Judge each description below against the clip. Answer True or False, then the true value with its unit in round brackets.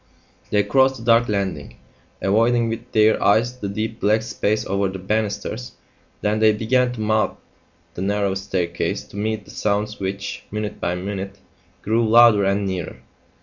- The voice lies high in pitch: False (105 Hz)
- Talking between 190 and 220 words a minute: False (160 wpm)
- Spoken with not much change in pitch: True (2.3 semitones)